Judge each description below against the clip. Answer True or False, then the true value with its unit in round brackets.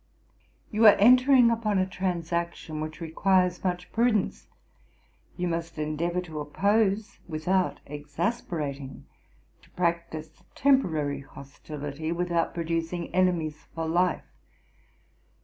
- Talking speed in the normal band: False (100 wpm)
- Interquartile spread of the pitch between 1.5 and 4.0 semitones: True (3.4 semitones)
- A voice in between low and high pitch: True (170 Hz)